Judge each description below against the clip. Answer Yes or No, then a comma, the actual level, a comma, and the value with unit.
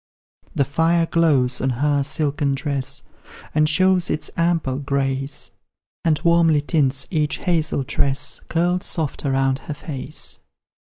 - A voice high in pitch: No, medium, 145 Hz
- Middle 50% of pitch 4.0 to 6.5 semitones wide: No, average, 3.2 semitones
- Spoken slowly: Yes, slow, 125 wpm